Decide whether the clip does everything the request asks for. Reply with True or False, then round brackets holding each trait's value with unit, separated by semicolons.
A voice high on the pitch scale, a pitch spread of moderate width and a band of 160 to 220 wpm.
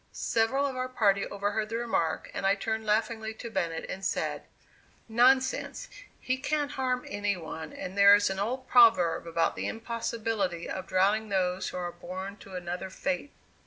True (210 Hz; 3.9 semitones; 170 wpm)